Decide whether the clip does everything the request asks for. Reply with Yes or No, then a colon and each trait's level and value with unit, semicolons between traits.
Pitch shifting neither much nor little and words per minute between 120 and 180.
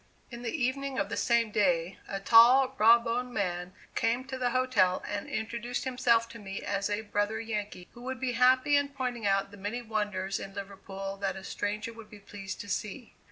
No: average, 3.7 semitones; fast, 205 wpm